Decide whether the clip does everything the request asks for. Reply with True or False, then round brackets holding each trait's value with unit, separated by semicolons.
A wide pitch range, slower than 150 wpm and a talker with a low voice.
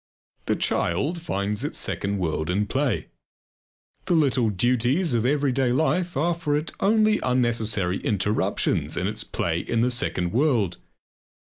True (6.7 semitones; 140 wpm; 120 Hz)